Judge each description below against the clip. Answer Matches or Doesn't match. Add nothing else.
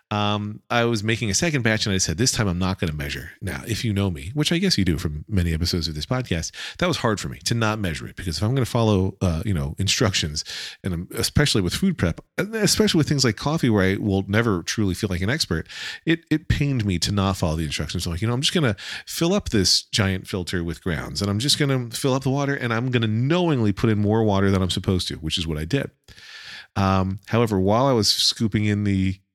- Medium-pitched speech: Doesn't match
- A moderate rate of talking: Doesn't match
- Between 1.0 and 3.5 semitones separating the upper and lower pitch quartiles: Doesn't match